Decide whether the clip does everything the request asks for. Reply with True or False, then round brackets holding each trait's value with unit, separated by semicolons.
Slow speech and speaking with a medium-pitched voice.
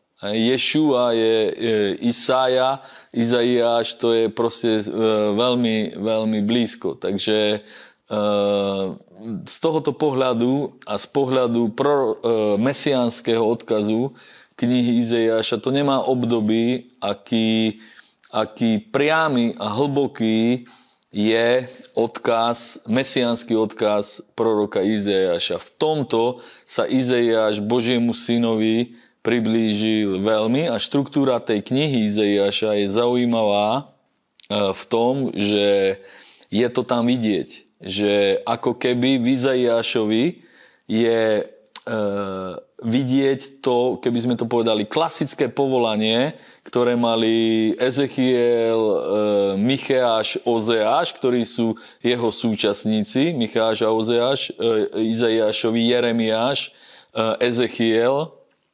False (90 wpm; 115 Hz)